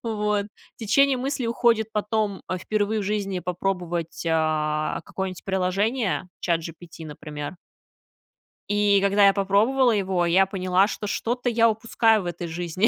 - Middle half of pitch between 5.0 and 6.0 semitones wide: No, average, 3.8 semitones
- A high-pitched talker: Yes, high, 195 Hz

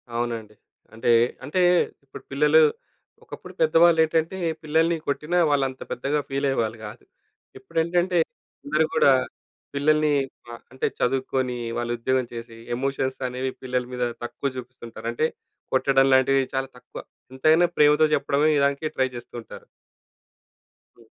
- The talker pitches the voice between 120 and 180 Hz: Yes, low, 135 Hz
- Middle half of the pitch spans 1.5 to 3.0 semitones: No, average, 3.4 semitones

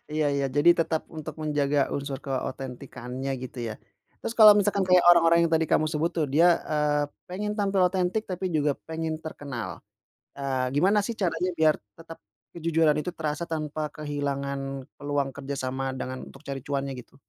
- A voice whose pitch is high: No, medium, 150 Hz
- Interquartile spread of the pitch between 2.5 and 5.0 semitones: Yes, average, 3.3 semitones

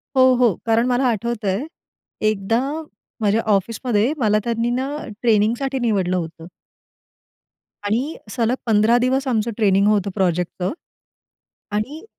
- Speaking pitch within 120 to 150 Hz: No, high, 225 Hz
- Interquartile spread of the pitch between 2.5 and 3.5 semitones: Yes, average, 3.2 semitones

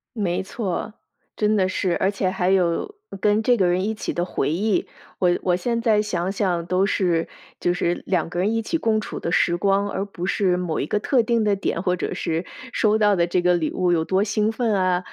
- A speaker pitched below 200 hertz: Yes, high, 190 Hz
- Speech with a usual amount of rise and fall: Yes, average, 3.0 semitones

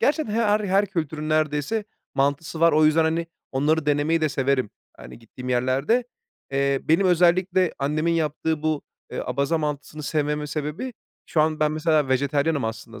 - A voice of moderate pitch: Yes, medium, 155 Hz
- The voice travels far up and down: No, average, 2.8 semitones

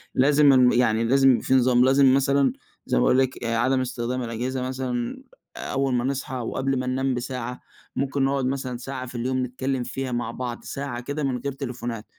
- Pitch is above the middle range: No, low, 130 Hz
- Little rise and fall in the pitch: Yes, narrow, 1.7 semitones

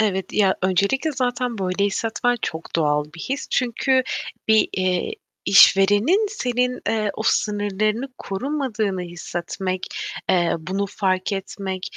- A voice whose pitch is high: Yes, high, 200 Hz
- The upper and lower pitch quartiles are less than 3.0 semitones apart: No, average, 4.7 semitones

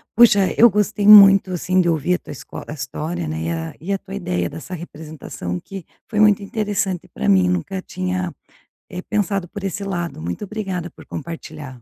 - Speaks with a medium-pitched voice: Yes, medium, 180 Hz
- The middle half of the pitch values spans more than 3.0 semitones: Yes, average, 4.6 semitones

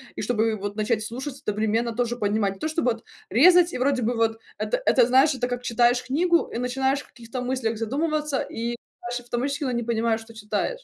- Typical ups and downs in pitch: Yes, average, 3.0 semitones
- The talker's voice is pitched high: Yes, high, 240 Hz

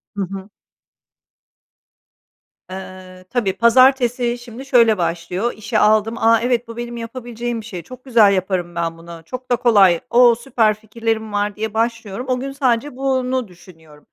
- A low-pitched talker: No, high, 225 Hz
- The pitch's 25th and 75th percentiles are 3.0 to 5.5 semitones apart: Yes, average, 4.1 semitones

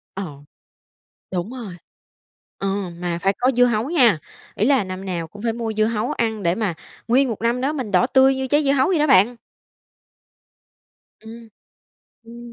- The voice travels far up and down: No, average, 4.7 semitones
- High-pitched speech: Yes, high, 230 Hz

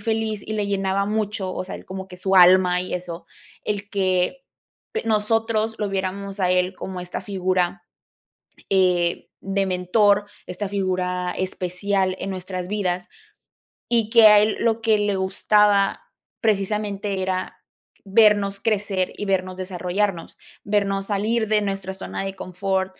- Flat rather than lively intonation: Yes, narrow, 2.0 semitones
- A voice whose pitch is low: No, high, 195 Hz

